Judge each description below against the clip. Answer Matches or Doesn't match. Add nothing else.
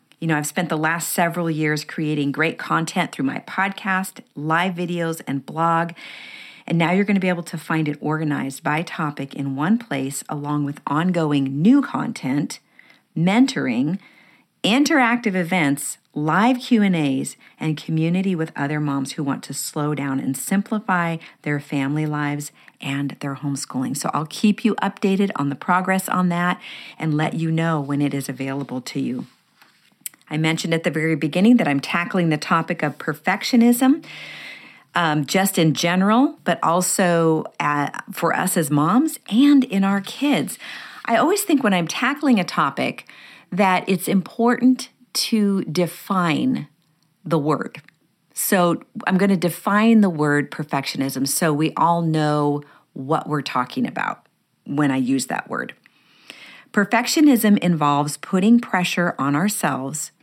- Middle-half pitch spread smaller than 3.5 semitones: Doesn't match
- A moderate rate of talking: Matches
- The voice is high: Doesn't match